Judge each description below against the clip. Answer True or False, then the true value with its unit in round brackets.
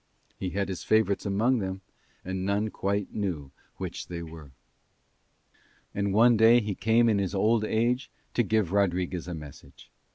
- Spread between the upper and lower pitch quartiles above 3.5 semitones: False (3.1 semitones)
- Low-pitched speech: True (100 Hz)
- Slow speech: False (160 wpm)